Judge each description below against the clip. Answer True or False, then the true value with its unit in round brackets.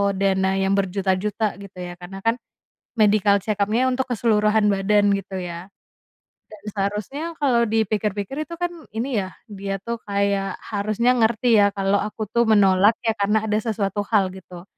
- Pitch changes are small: True (2.2 semitones)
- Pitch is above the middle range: True (205 Hz)